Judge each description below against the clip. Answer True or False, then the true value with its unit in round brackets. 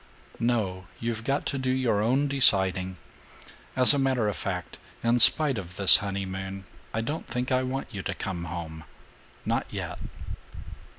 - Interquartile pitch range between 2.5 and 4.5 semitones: False (5.2 semitones)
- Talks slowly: False (160 wpm)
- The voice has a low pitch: True (110 Hz)